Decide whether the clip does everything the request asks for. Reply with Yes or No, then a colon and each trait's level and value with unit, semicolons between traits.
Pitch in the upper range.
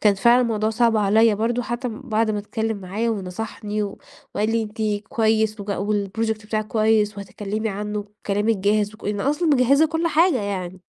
Yes: high, 215 Hz